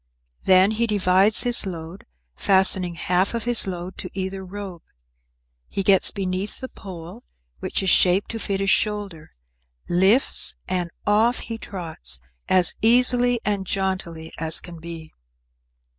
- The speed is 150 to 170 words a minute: No, average, 140 wpm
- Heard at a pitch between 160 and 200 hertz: Yes, high, 190 Hz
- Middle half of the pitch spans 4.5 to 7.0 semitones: No, average, 2.9 semitones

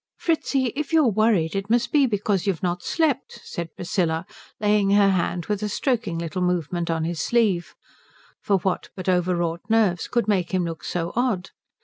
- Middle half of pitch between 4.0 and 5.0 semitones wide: Yes, average, 4.4 semitones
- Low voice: No, high, 190 Hz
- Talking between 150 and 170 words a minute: No, average, 185 wpm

